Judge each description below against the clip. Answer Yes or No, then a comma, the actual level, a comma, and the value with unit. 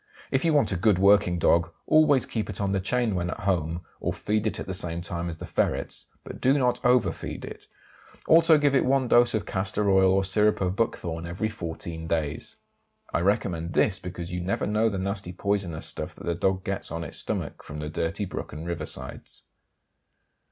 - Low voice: Yes, very low, 95 Hz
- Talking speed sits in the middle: No, fast, 210 wpm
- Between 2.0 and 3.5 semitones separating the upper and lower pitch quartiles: No, average, 4.1 semitones